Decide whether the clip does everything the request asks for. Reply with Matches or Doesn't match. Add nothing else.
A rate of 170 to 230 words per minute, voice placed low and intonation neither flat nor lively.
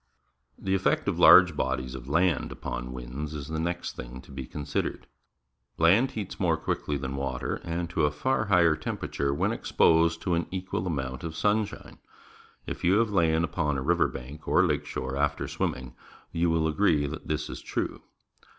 Matches